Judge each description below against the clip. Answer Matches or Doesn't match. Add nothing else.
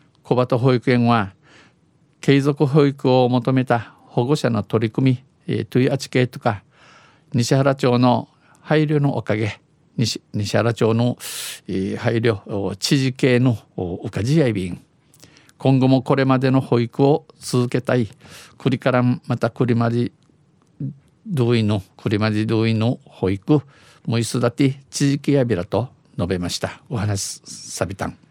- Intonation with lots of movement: Doesn't match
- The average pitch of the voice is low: Matches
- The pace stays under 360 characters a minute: Matches